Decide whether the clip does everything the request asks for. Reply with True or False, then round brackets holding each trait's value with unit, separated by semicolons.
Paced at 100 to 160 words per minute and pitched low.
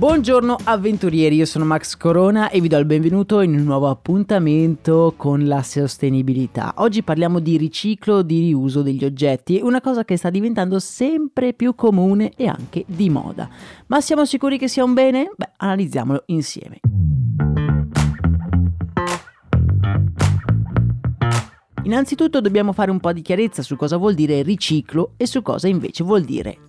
False (150 wpm; 170 Hz)